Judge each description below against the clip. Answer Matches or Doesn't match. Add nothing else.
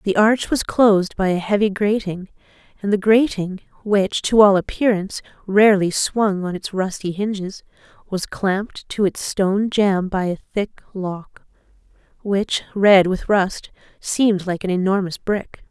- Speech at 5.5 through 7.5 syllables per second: Doesn't match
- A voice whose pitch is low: Doesn't match